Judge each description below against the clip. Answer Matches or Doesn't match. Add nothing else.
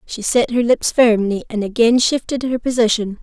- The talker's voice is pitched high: Matches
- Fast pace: Doesn't match